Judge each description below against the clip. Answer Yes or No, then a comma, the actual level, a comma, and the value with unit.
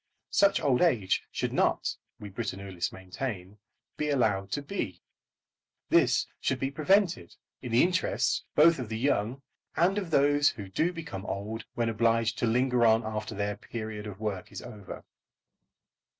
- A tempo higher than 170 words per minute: No, average, 155 wpm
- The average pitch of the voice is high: No, low, 115 Hz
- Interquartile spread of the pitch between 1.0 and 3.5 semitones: No, wide, 5.6 semitones